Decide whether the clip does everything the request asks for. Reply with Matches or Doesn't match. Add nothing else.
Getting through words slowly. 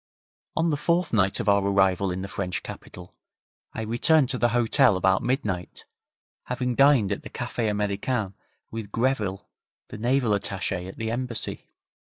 Doesn't match